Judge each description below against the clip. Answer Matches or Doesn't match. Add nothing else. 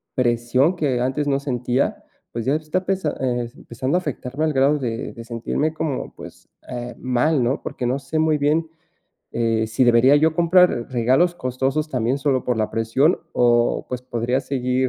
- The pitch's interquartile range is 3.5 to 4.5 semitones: Matches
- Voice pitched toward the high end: Doesn't match